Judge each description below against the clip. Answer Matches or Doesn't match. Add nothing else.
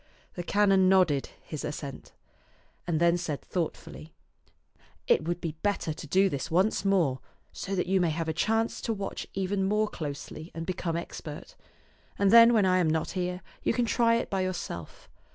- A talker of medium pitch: Matches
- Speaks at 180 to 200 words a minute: Matches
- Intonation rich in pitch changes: Doesn't match